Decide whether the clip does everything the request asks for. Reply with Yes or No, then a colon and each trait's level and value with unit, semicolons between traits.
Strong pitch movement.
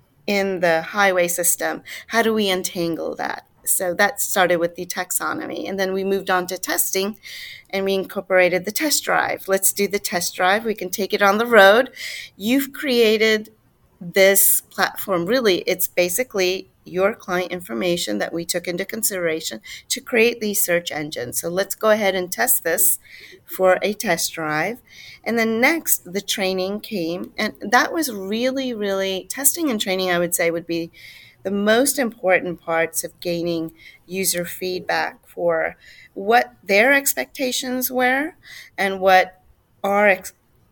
No: average, 3.6 semitones